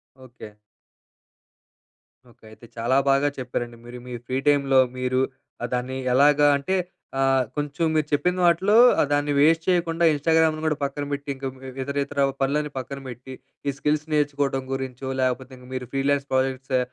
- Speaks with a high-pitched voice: No, medium, 140 Hz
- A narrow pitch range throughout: Yes, narrow, 2.3 semitones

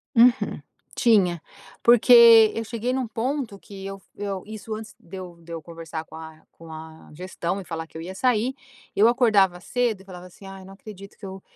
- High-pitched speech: Yes, high, 195 Hz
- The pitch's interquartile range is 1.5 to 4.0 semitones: No, average, 4.5 semitones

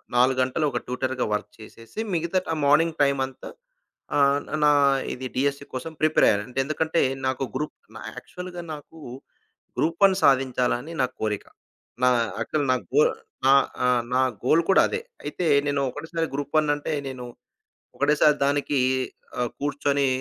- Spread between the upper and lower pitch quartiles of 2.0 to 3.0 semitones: No, average, 3.6 semitones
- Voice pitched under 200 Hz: Yes, medium, 140 Hz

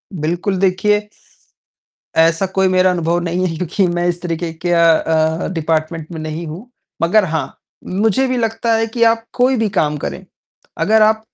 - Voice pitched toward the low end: No, medium, 180 Hz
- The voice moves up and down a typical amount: Yes, average, 4.7 semitones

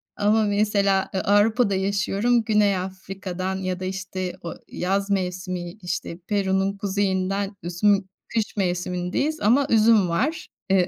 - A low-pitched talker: No, high, 195 Hz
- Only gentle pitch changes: Yes, narrow, 1.9 semitones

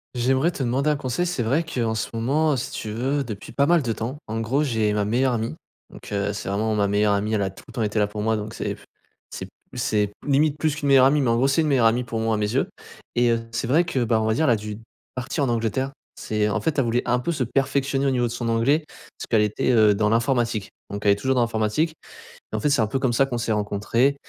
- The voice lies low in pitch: Yes, low, 120 Hz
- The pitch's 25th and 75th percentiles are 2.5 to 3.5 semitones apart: No, average, 3.9 semitones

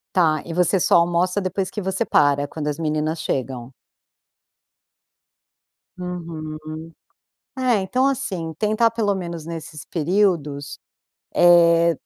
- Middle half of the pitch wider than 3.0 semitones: Yes, average, 3.5 semitones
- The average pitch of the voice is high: No, medium, 170 Hz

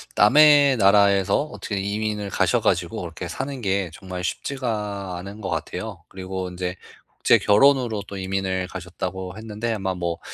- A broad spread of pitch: No, average, 2.8 semitones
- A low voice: Yes, low, 100 Hz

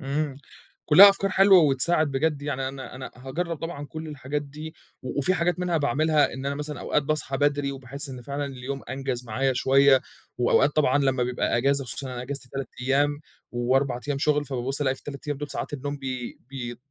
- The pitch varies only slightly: Yes, narrow, 2.1 semitones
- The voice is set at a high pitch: No, medium, 140 Hz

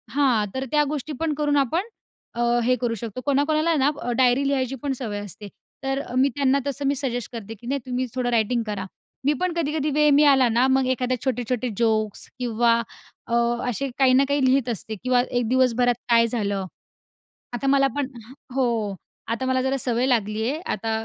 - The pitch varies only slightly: No, average, 3.0 semitones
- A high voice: Yes, very high, 255 Hz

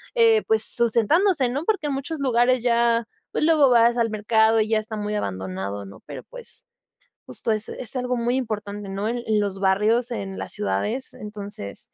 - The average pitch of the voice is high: Yes, high, 225 Hz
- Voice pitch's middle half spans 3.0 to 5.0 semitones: Yes, average, 3.5 semitones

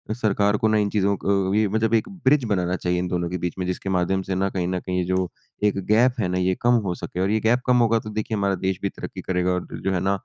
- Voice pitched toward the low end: Yes, very low, 95 Hz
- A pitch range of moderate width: Yes, average, 3.0 semitones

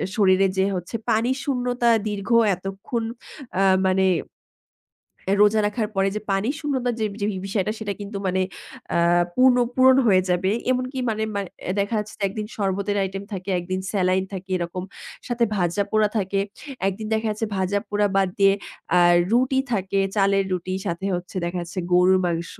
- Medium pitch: No, high, 200 Hz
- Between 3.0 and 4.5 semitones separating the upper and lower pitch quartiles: No, narrow, 2.6 semitones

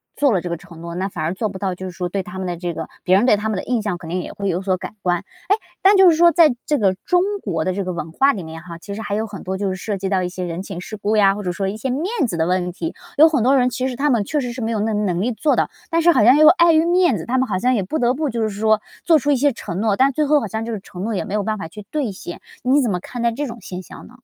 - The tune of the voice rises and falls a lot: Yes, wide, 5.8 semitones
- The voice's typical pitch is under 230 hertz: Yes, high, 210 Hz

